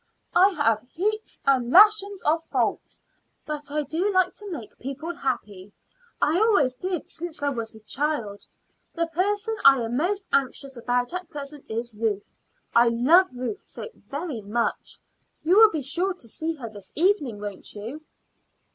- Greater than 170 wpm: No, average, 165 wpm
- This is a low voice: No, very high, 290 Hz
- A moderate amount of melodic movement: No, wide, 7.2 semitones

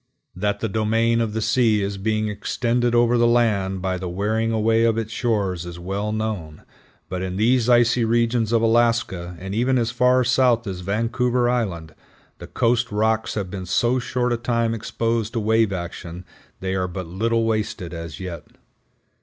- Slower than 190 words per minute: Yes, average, 180 wpm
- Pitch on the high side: No, low, 110 Hz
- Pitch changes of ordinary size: Yes, average, 3.7 semitones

